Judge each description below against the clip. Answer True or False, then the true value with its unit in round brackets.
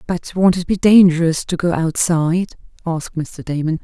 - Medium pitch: True (170 Hz)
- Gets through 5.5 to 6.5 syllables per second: False (5.1 syllables/s)